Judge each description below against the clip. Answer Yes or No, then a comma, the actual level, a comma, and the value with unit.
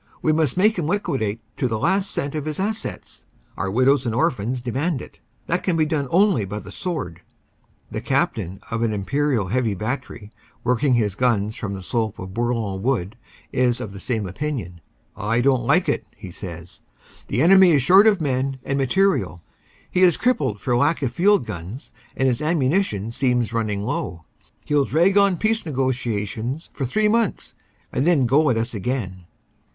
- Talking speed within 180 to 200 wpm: Yes, average, 185 wpm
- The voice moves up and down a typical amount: No, wide, 6.6 semitones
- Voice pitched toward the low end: Yes, low, 130 Hz